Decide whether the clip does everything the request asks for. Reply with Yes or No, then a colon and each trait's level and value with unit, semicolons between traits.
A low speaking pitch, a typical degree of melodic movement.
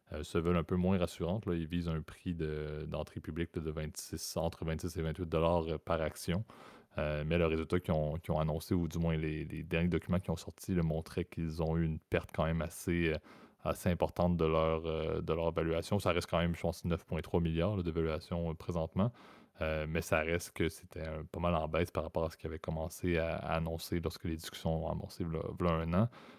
No: very low, 85 Hz; narrow, 1.6 semitones